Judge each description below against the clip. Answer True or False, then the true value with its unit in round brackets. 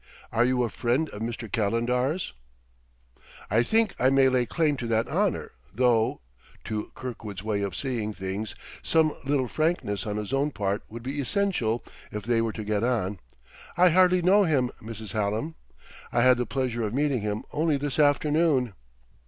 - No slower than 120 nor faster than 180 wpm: True (170 wpm)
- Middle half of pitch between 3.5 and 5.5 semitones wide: True (5.0 semitones)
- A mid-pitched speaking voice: False (120 Hz)